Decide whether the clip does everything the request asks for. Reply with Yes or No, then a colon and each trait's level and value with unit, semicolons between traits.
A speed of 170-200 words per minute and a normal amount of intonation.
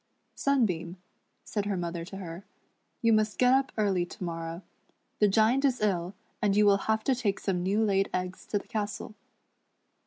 Yes: average, 180 wpm; average, 3.2 semitones